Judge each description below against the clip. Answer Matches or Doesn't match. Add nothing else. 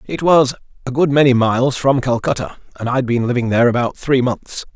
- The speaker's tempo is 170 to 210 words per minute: Matches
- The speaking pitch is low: Matches